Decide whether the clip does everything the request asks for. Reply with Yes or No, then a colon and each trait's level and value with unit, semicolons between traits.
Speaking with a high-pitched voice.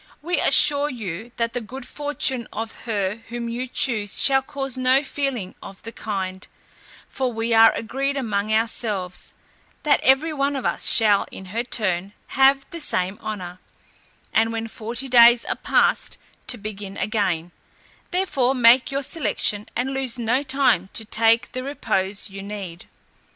Yes: high, 230 Hz